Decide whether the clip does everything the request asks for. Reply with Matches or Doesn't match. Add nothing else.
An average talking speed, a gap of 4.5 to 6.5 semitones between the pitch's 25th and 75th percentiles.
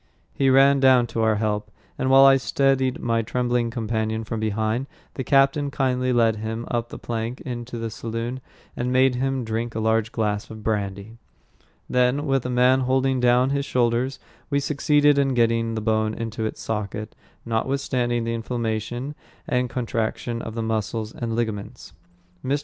Doesn't match